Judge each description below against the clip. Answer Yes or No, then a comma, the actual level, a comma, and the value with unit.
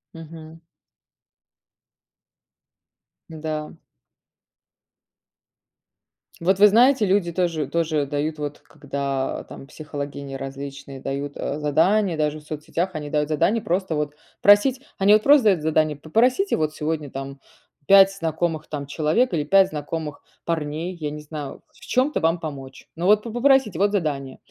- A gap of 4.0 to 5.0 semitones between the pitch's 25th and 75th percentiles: Yes, average, 4.7 semitones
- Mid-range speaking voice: Yes, medium, 155 Hz